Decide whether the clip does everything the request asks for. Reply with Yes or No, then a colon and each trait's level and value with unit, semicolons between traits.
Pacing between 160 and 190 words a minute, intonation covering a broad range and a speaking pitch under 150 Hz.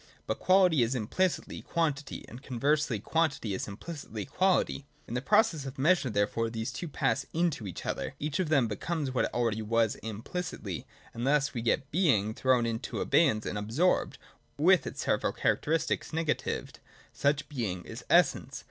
Yes: average, 165 wpm; wide, 6.0 semitones; low, 135 Hz